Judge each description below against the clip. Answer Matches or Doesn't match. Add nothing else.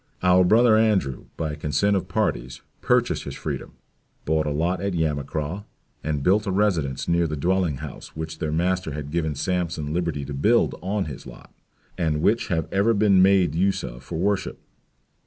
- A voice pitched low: Matches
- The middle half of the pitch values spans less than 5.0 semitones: Matches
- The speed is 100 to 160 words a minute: Doesn't match